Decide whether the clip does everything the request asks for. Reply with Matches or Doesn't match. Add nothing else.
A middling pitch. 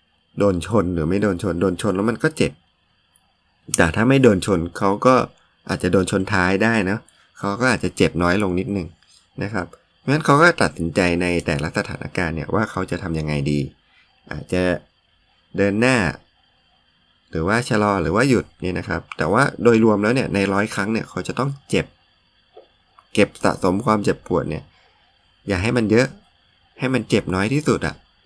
Doesn't match